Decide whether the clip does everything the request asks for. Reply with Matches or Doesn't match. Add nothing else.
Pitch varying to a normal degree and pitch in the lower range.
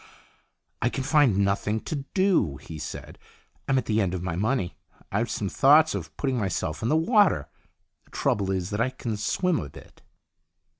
Doesn't match